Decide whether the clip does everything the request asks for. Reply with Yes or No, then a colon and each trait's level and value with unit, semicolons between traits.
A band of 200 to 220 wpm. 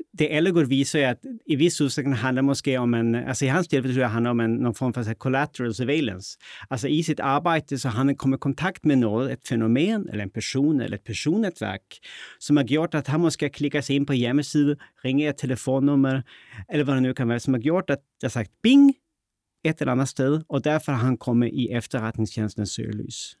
Yes: average, 210 wpm